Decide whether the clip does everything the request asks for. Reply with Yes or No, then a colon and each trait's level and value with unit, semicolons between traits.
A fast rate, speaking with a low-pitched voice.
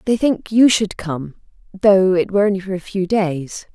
No: fast, 210 wpm; high, 190 Hz